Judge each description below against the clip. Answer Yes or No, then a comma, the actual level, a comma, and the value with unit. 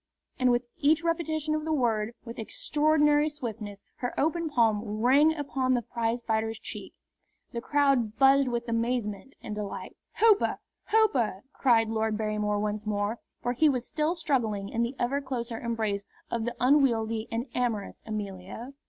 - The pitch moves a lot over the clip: No, average, 4.4 semitones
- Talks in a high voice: Yes, high, 240 Hz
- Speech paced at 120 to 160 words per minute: Yes, average, 155 wpm